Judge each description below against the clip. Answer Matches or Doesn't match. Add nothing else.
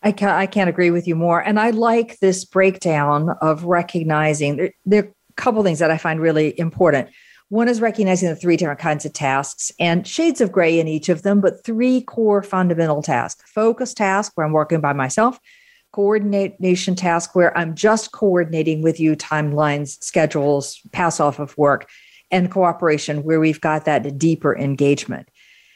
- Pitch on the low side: Doesn't match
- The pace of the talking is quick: Doesn't match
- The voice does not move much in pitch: Doesn't match